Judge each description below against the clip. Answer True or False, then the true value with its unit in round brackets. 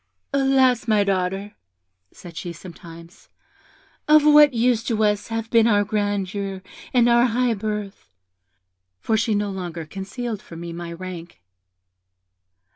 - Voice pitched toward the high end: True (205 Hz)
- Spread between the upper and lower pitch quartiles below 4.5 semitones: True (4.1 semitones)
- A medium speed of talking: False (130 wpm)